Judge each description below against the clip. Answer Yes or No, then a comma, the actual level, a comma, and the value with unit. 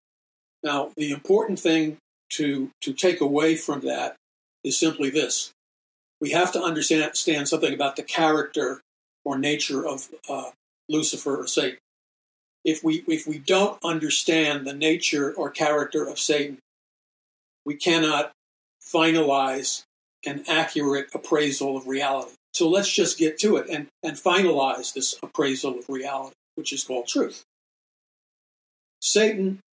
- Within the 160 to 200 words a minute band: No, slow, 135 wpm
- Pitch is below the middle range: No, medium, 155 Hz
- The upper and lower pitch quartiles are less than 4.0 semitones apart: Yes, average, 2.8 semitones